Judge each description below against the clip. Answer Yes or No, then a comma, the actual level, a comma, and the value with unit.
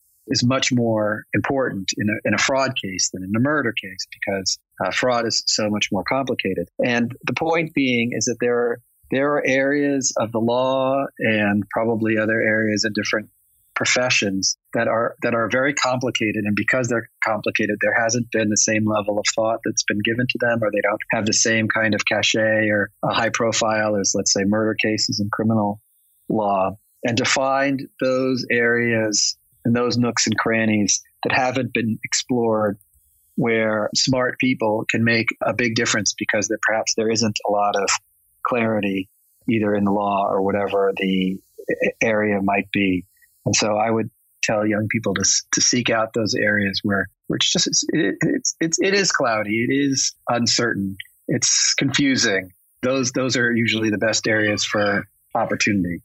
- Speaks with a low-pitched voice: Yes, low, 110 Hz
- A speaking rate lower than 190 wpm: Yes, average, 175 wpm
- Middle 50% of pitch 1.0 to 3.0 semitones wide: Yes, average, 2.7 semitones